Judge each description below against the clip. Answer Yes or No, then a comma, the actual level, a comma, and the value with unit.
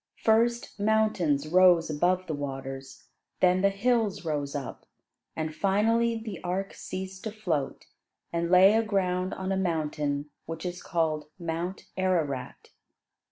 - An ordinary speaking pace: No, slow, 130 wpm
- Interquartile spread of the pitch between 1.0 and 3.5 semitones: No, average, 4.2 semitones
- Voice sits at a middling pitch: Yes, medium, 180 Hz